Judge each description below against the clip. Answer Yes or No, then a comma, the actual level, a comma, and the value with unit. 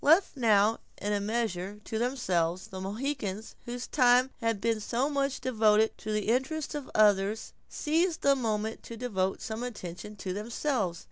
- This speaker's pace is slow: No, average, 160 wpm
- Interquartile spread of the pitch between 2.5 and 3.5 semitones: No, average, 4.0 semitones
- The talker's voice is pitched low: No, high, 225 Hz